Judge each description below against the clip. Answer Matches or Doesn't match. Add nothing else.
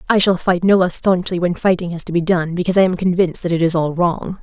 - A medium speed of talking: Doesn't match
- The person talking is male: Doesn't match